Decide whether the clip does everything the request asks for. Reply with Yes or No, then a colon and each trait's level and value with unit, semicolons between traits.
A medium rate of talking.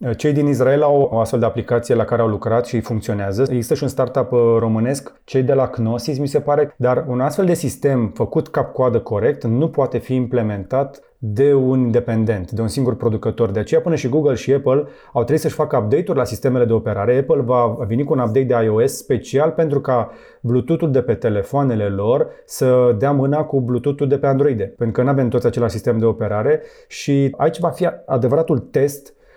No: fast, 205 wpm